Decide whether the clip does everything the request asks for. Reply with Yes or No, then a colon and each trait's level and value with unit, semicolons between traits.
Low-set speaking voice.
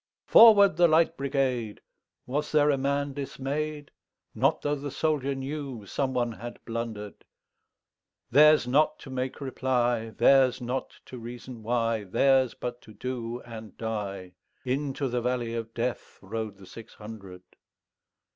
Yes: low, 125 Hz